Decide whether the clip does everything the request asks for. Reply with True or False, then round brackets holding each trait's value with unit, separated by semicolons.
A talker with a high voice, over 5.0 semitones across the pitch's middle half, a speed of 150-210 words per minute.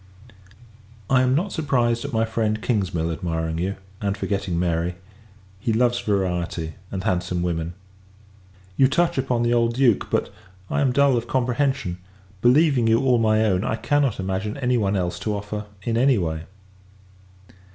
False (110 Hz; 5.4 semitones; 160 wpm)